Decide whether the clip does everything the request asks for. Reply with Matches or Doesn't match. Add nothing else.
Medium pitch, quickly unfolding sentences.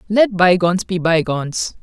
Doesn't match